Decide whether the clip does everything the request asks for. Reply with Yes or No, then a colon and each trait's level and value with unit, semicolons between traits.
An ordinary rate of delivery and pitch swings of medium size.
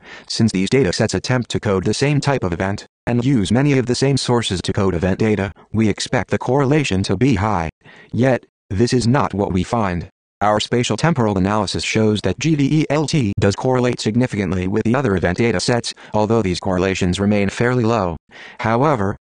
Yes: average, 180 wpm; average, 4.6 semitones